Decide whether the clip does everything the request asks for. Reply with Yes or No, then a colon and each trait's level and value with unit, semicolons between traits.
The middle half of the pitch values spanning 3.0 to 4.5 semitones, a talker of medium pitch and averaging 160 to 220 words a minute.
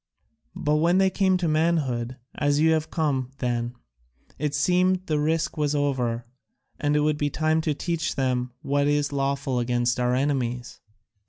Yes: average, 3.7 semitones; medium, 145 Hz; average, 165 wpm